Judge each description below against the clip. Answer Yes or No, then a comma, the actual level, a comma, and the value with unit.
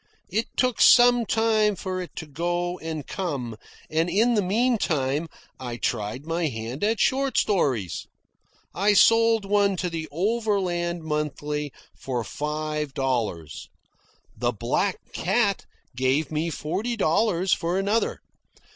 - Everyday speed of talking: No, slow, 130 wpm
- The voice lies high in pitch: No, medium, 175 Hz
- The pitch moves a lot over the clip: Yes, wide, 5.9 semitones